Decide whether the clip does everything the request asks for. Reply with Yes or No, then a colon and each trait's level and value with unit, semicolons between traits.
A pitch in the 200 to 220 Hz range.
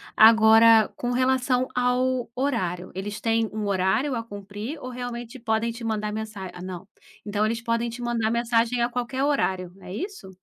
No: high, 230 Hz